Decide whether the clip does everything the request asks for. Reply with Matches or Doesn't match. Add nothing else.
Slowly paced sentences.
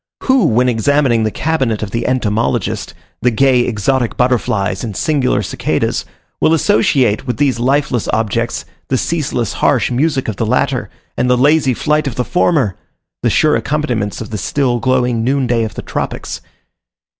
Doesn't match